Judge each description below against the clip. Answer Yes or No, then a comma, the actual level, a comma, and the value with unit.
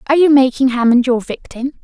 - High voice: Yes, very high, 260 Hz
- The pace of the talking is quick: No, average, 195 wpm